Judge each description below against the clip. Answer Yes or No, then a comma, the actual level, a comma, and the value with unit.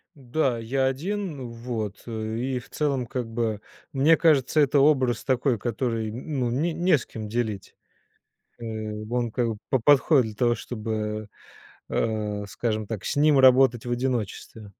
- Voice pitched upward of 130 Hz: No, low, 120 Hz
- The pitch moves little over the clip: No, average, 3.3 semitones